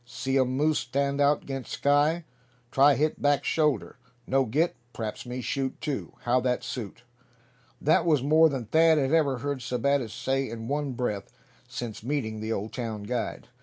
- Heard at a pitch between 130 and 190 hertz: Yes, low, 135 Hz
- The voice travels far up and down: No, average, 3.2 semitones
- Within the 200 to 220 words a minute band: No, average, 170 wpm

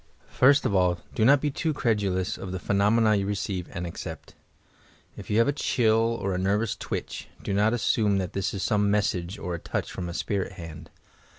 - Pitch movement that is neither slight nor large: Yes, average, 3.3 semitones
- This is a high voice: No, low, 100 Hz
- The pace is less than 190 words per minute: No, fast, 205 wpm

